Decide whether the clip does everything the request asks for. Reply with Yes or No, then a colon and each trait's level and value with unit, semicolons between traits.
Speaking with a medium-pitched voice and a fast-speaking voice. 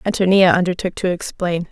No: medium, 180 Hz; average, 140 wpm